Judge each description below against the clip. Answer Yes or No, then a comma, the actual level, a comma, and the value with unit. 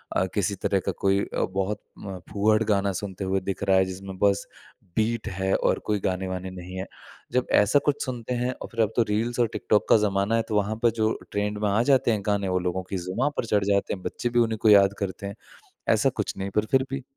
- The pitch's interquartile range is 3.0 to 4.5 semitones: No, narrow, 2.6 semitones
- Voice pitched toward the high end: No, low, 100 Hz